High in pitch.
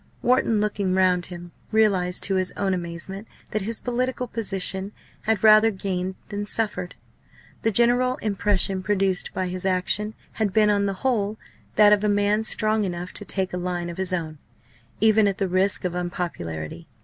Yes: high, 195 Hz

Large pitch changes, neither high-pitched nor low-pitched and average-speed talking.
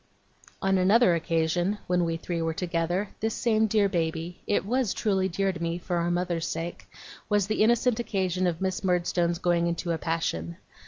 No: average, 2.8 semitones; medium, 180 Hz; average, 180 wpm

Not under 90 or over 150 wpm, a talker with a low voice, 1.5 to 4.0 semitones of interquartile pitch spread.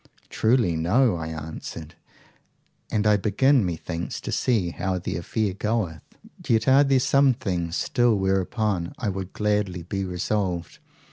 No: average, 140 wpm; low, 100 Hz; average, 4.4 semitones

